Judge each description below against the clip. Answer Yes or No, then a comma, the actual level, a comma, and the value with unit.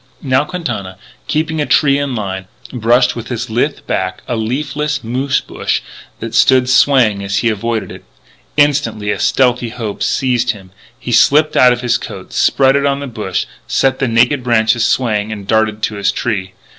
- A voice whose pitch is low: Yes, low, 120 Hz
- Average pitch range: Yes, average, 3.9 semitones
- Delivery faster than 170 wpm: Yes, average, 180 wpm